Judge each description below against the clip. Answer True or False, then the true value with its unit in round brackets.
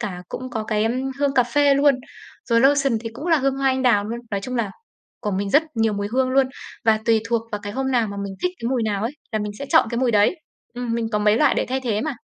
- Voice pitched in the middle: False (235 Hz)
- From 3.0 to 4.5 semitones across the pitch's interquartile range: True (3.9 semitones)